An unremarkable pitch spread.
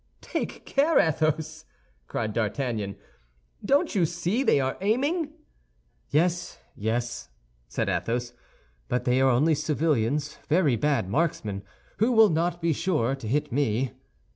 No: wide, 6.2 semitones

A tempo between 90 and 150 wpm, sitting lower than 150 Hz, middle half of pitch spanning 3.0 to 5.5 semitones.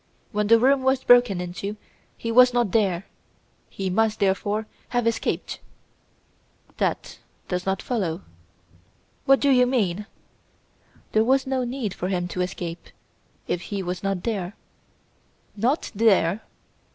No: slow, 135 wpm; high, 210 Hz; average, 4.8 semitones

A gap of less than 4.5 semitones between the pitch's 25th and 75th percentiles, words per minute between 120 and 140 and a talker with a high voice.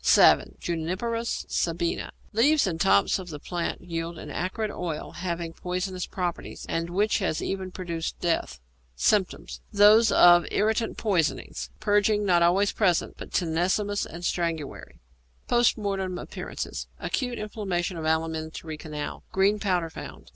No: average, 3.7 semitones; slow, 135 wpm; medium, 180 Hz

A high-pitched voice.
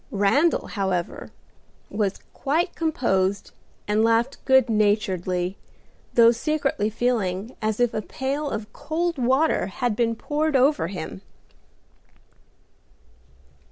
Yes: high, 230 Hz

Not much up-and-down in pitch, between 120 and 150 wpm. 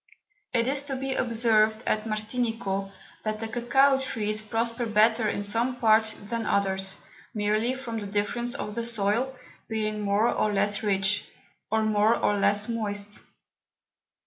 Yes: narrow, 2.2 semitones; average, 145 wpm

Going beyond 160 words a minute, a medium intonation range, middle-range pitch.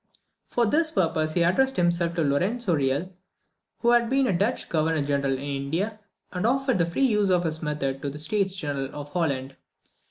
No: average, 190 wpm; wide, 6.6 semitones; medium, 170 Hz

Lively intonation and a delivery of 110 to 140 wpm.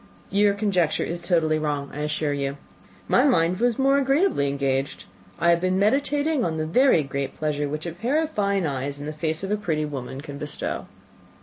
No: wide, 6.1 semitones; average, 200 wpm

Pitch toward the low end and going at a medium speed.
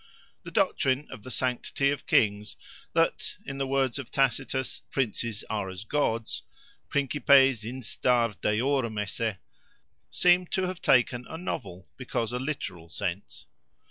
No: low, 125 Hz; slow, 125 wpm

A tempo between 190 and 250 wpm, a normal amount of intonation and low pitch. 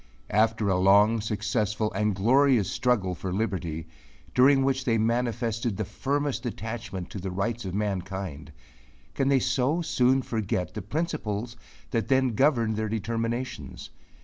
No: average, 140 wpm; average, 4.1 semitones; low, 110 Hz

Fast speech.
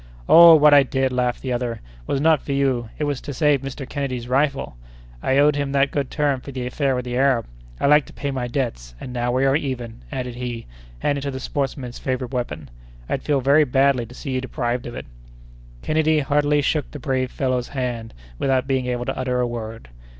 Yes: fast, 220 wpm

